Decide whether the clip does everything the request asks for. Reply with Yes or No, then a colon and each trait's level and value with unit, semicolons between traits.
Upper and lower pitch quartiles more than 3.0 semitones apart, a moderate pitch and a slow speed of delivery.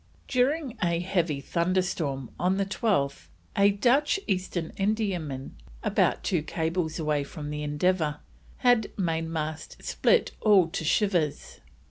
Yes: average, 4.4 semitones; medium, 175 Hz; slow, 120 wpm